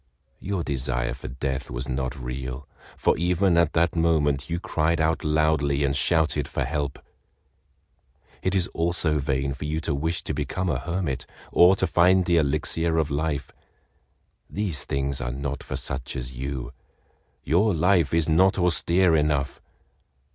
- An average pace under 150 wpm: No, average, 155 wpm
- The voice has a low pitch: Yes, very low, 75 Hz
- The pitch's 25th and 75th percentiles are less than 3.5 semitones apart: No, average, 3.8 semitones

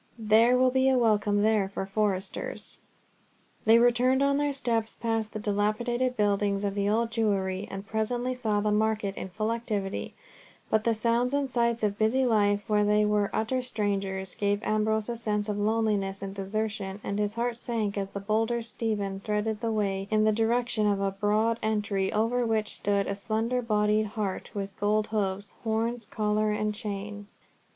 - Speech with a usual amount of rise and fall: No, narrow, 2.0 semitones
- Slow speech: No, average, 175 wpm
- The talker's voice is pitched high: Yes, high, 215 Hz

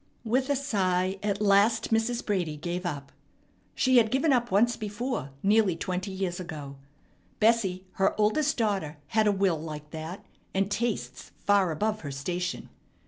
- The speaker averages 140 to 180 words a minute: Yes, average, 155 wpm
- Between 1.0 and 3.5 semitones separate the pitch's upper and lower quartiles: No, average, 4.1 semitones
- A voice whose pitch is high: Yes, high, 195 Hz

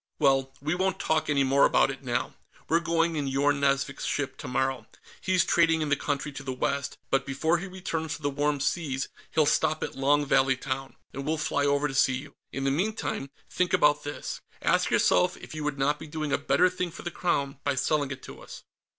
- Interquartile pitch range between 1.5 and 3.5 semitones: Yes, average, 2.7 semitones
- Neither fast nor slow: No, fast, 220 wpm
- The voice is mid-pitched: Yes, medium, 145 Hz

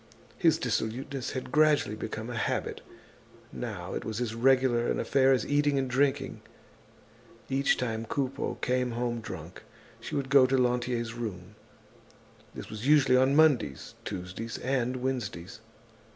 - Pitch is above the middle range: No, low, 125 Hz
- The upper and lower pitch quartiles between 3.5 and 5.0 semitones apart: No, average, 2.8 semitones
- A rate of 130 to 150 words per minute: Yes, average, 140 wpm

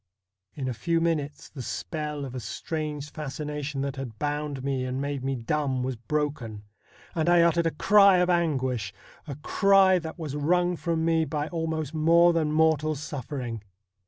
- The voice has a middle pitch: Yes, medium, 150 Hz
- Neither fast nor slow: Yes, average, 175 wpm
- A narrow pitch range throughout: No, average, 3.4 semitones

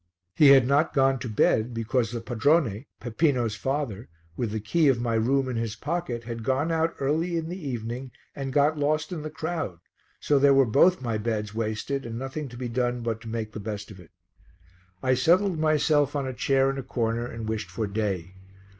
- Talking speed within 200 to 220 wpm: Yes, fast, 205 wpm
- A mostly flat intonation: No, average, 4.3 semitones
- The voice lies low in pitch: Yes, low, 130 Hz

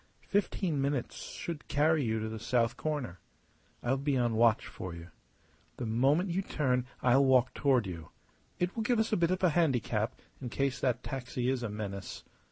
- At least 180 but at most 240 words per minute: Yes, average, 185 wpm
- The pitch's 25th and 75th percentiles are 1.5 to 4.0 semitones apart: No, average, 4.8 semitones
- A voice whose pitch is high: No, low, 130 Hz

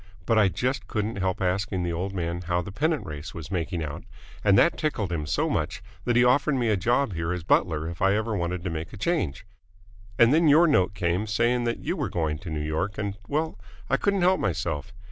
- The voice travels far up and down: Yes, wide, 6.0 semitones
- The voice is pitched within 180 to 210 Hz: No, very low, 95 Hz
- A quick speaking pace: Yes, fast, 230 wpm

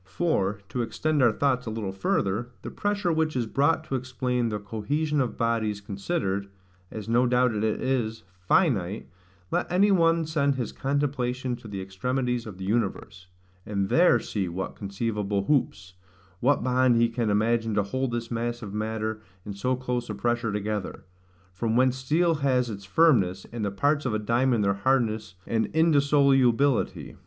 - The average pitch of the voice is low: Yes, low, 120 Hz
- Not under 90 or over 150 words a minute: No, average, 175 wpm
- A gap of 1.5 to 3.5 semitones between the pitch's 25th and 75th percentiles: No, average, 4.2 semitones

